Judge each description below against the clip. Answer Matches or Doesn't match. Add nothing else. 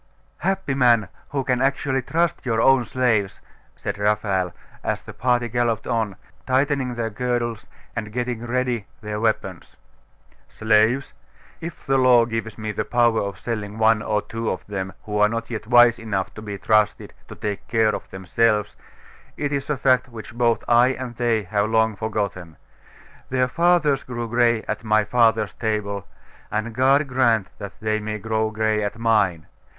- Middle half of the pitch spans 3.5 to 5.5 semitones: Doesn't match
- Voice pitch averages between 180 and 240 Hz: Doesn't match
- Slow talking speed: Doesn't match